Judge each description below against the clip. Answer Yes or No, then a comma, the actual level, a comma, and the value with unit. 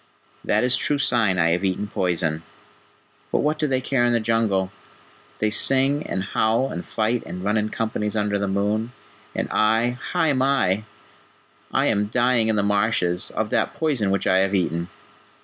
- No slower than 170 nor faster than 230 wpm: Yes, average, 180 wpm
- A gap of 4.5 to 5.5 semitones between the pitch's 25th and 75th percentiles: No, average, 4.0 semitones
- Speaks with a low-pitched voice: Yes, low, 110 Hz